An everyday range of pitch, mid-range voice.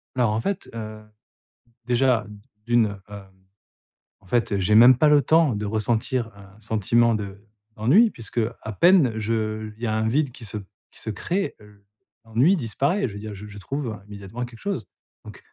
No: average, 3.3 semitones; low, 110 Hz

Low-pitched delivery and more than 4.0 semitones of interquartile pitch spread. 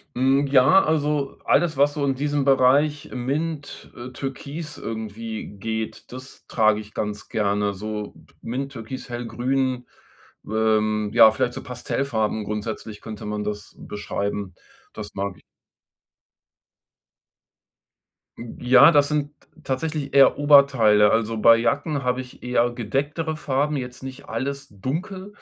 Yes: low, 125 Hz; average, 4.5 semitones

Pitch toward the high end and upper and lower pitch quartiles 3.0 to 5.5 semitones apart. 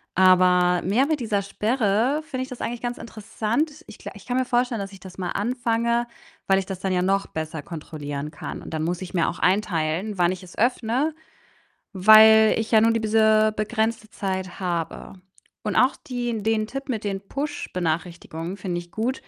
Yes: high, 210 Hz; average, 4.4 semitones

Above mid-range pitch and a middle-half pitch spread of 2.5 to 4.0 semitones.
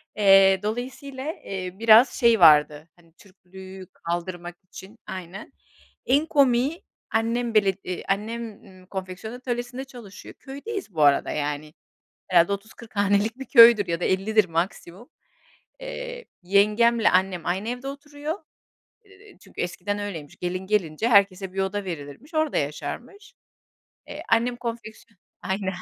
No: high, 205 Hz; average, 4.8 semitones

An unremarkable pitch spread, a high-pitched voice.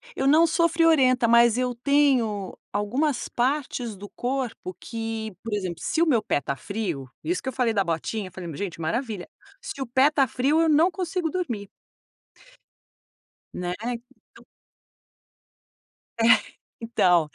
No: wide, 5.8 semitones; high, 240 Hz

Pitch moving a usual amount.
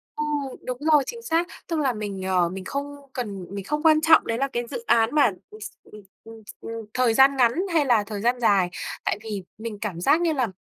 No: wide, 5.7 semitones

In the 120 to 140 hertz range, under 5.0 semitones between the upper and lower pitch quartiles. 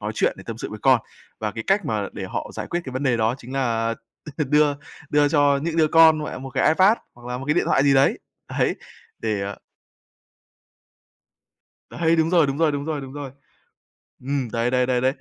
Yes: low, 135 Hz; average, 3.8 semitones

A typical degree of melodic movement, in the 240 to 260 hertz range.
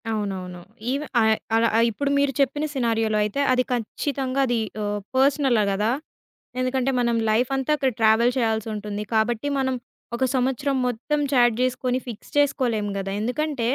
Yes: average, 3.4 semitones; high, 245 Hz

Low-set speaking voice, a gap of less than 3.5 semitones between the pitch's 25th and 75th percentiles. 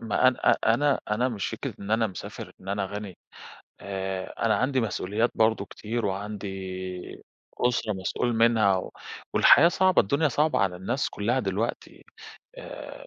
No: low, 110 Hz; average, 3.8 semitones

